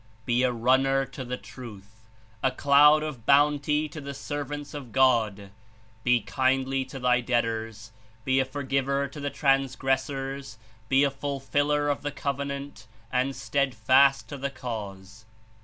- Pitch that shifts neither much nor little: No, narrow, 2.2 semitones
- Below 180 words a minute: Yes, average, 140 wpm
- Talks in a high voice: No, low, 135 Hz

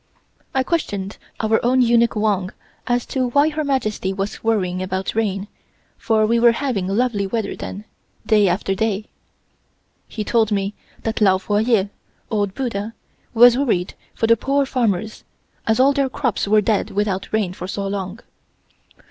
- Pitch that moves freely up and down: No, average, 3.4 semitones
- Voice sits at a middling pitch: No, high, 215 Hz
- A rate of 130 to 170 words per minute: Yes, average, 160 wpm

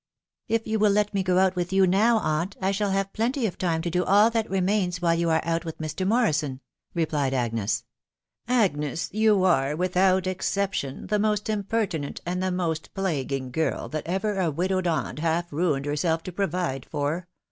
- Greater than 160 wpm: Yes, average, 190 wpm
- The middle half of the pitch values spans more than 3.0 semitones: Yes, average, 3.8 semitones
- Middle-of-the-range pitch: Yes, medium, 180 Hz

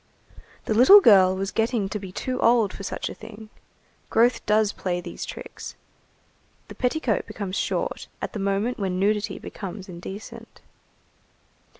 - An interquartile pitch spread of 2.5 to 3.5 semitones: Yes, average, 3.0 semitones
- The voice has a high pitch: Yes, high, 210 Hz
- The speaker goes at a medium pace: Yes, average, 150 wpm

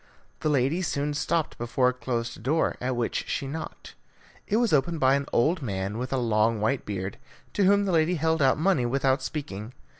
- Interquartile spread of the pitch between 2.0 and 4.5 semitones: No, average, 5.2 semitones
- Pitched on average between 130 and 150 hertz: Yes, low, 135 Hz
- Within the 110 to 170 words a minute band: No, average, 200 wpm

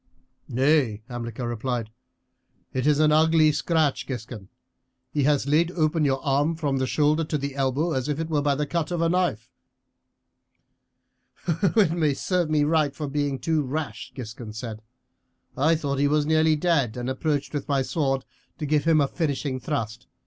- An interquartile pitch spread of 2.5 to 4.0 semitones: Yes, average, 3.1 semitones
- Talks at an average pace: Yes, average, 170 wpm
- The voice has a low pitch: No, medium, 145 Hz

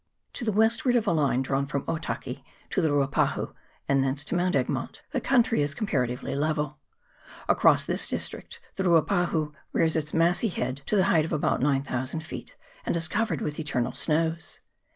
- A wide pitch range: No, average, 4.1 semitones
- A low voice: No, medium, 155 Hz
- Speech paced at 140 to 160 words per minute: No, average, 175 wpm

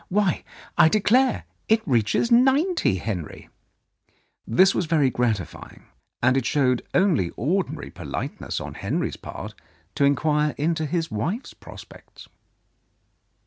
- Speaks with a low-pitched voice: No, medium, 155 Hz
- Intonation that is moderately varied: No, wide, 8.2 semitones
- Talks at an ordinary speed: No, slow, 120 wpm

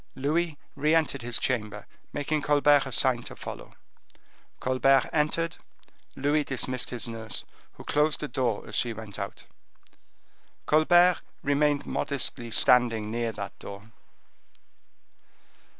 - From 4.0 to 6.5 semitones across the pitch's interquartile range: Yes, average, 4.4 semitones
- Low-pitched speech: Yes, low, 130 Hz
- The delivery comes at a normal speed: No, slow, 120 wpm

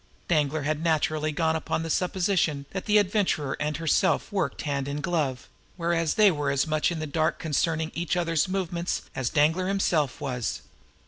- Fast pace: No, average, 175 wpm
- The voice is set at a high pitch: No, medium, 160 Hz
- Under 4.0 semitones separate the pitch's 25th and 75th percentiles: Yes, average, 2.9 semitones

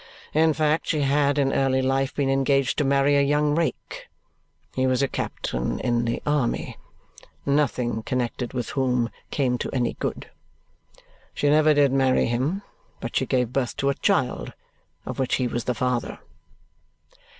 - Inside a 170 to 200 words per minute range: No, average, 160 wpm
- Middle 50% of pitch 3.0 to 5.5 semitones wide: No, narrow, 2.6 semitones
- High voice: No, low, 135 Hz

